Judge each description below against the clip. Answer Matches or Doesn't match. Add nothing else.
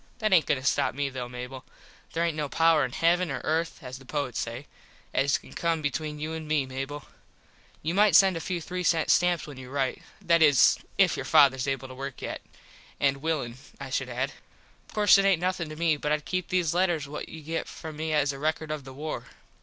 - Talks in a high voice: Doesn't match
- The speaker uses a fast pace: Matches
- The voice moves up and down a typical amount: Matches